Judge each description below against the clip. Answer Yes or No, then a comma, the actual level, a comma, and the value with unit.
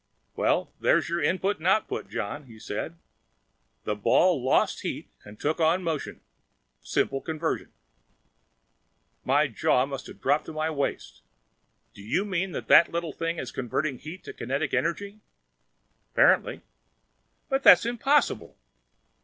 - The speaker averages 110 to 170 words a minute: Yes, slow, 135 wpm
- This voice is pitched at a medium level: Yes, medium, 160 Hz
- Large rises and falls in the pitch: No, average, 5.0 semitones